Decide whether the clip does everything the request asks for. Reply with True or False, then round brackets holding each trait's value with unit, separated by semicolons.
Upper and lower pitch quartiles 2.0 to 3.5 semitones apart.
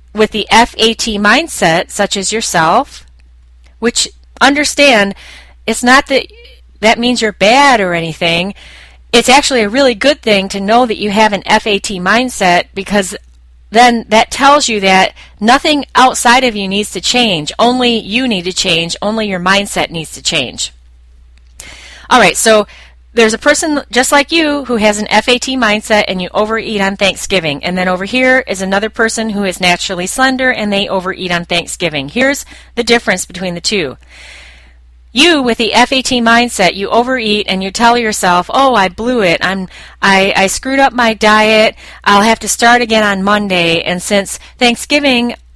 False (4.7 semitones)